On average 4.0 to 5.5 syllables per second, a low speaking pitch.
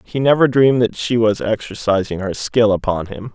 Yes: 5.2 syllables/s; low, 110 Hz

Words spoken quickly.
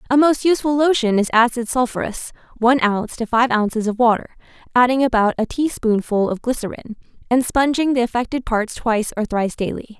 No: average, 175 wpm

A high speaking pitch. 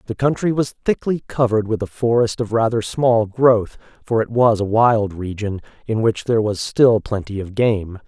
No: low, 110 Hz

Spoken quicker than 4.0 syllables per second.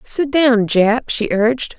No: 3.7 syllables/s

